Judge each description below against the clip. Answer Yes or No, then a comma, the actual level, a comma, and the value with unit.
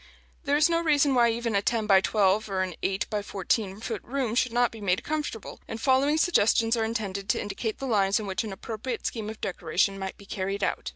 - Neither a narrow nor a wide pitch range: Yes, average, 3.7 semitones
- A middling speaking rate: No, fast, 235 wpm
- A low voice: No, high, 220 Hz